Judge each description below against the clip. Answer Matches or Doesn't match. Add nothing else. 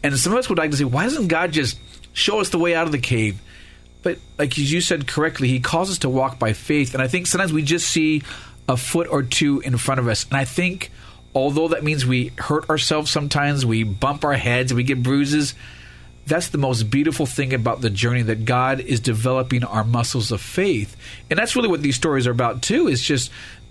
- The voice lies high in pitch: Doesn't match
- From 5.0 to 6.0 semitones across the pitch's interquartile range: Doesn't match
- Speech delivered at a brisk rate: Matches